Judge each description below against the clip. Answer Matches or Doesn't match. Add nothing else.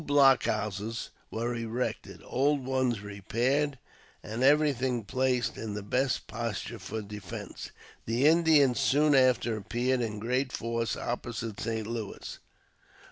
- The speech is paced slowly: Matches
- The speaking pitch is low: Matches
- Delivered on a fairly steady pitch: Doesn't match